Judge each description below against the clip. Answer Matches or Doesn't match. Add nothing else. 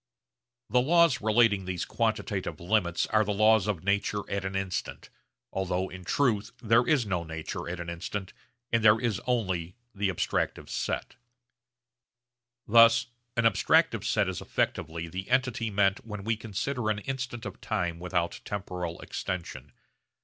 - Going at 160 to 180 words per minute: Doesn't match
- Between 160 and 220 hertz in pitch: Doesn't match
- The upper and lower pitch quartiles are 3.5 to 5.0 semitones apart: Matches